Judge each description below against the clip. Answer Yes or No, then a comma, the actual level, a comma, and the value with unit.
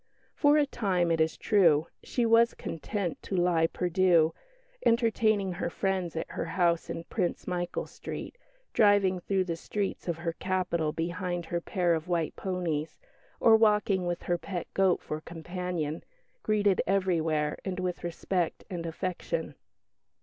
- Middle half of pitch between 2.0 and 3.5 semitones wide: Yes, average, 2.7 semitones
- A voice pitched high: No, medium, 180 Hz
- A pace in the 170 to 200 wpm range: No, average, 145 wpm